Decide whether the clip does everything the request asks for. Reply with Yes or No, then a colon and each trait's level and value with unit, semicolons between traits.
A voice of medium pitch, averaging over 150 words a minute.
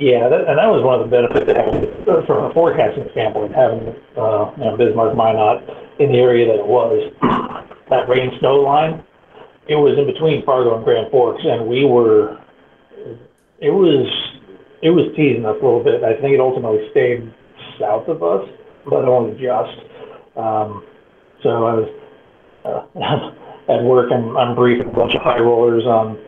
No: low, 125 Hz; average, 175 wpm